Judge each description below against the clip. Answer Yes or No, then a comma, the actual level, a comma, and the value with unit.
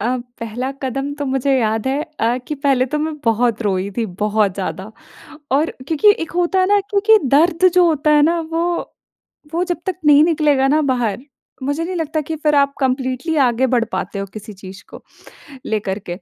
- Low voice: No, very high, 275 Hz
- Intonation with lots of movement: Yes, wide, 5.7 semitones